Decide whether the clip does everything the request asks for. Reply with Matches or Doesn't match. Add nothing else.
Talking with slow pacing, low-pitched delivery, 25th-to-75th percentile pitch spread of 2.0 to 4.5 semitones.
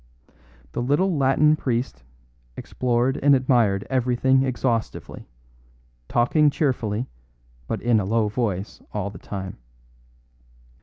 Matches